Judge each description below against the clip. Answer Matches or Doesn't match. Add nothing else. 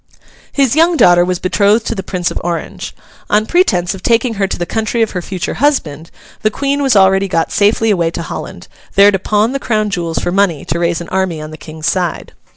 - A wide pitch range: Doesn't match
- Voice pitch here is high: Matches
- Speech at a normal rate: Doesn't match